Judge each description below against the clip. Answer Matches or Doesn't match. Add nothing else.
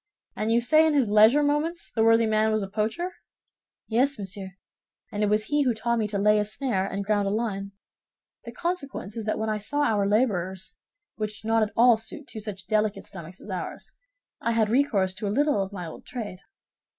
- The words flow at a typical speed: Doesn't match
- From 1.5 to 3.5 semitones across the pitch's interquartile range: Matches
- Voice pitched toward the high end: Matches